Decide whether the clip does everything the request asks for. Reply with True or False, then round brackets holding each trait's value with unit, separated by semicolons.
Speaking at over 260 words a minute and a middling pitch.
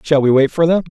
True (315 wpm; 150 Hz)